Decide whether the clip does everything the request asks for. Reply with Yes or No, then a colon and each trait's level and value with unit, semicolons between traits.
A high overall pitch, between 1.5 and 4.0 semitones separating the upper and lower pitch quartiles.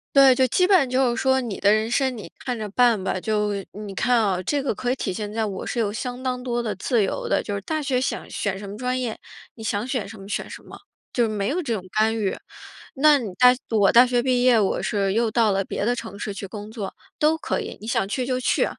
Yes: high, 230 Hz; average, 3.6 semitones